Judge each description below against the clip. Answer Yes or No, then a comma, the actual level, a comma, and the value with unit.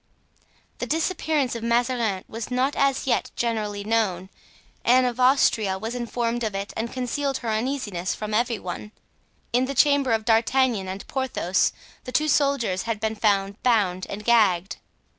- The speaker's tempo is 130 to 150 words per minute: No, average, 160 wpm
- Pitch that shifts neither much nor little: Yes, average, 3.7 semitones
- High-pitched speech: Yes, high, 230 Hz